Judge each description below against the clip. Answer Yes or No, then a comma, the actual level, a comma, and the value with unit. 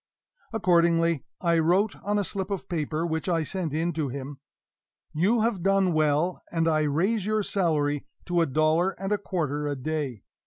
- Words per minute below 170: No, average, 180 wpm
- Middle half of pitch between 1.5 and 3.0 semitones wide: No, average, 3.7 semitones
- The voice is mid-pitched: Yes, medium, 165 Hz